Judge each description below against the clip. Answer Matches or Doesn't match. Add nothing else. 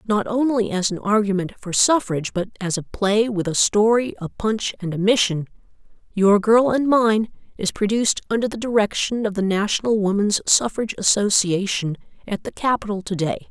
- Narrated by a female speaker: Matches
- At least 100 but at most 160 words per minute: Doesn't match